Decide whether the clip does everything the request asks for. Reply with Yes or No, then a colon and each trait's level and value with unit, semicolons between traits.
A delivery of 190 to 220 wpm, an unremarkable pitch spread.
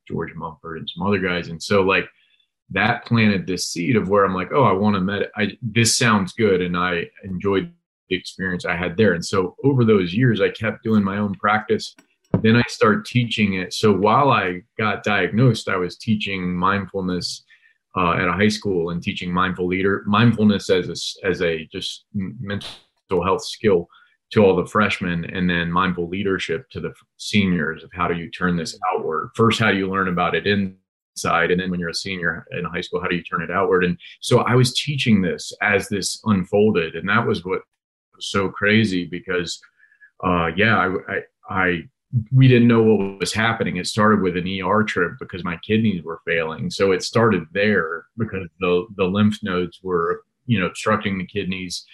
Yes: average, 200 wpm; average, 3.4 semitones